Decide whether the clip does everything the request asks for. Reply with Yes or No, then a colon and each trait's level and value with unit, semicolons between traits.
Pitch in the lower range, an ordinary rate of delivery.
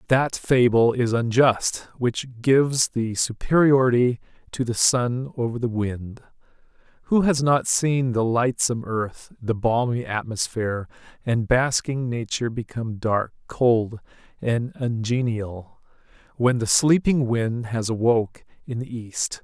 No: low, 120 Hz; slow, 125 wpm